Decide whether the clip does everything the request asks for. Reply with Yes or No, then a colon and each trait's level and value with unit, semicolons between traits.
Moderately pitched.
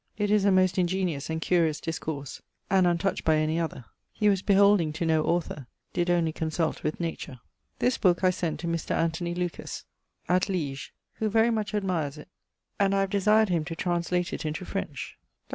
Yes: medium, 175 Hz